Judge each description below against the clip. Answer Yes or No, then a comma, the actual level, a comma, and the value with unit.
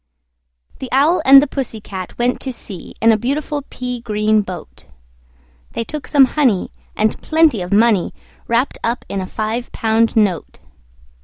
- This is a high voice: Yes, high, 230 Hz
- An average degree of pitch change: Yes, average, 4.1 semitones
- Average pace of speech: Yes, average, 160 wpm